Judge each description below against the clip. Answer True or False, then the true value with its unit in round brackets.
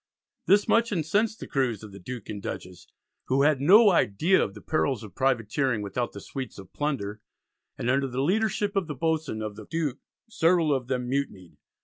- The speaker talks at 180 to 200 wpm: True (195 wpm)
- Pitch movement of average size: False (6.9 semitones)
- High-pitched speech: False (135 Hz)